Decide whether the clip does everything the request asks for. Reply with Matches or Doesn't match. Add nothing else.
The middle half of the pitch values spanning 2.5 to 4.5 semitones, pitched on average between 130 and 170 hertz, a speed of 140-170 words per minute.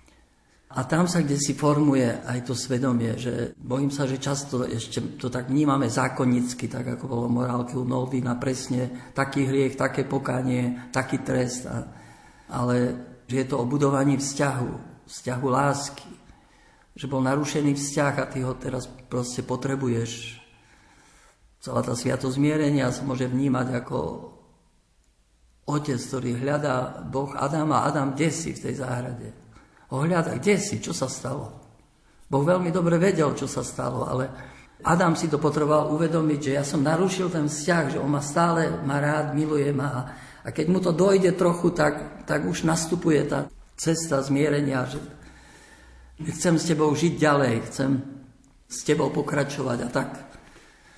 Matches